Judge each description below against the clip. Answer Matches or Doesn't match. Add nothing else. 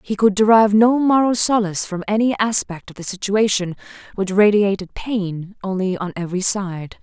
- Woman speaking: Matches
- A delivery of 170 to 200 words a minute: Doesn't match